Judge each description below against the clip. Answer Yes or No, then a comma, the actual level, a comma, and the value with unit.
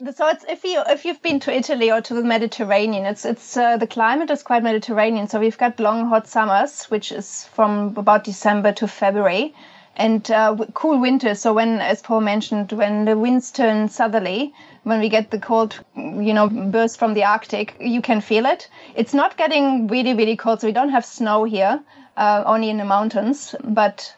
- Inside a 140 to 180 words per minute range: No, average, 200 wpm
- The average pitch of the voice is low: No, high, 225 Hz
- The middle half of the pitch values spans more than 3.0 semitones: No, narrow, 2.6 semitones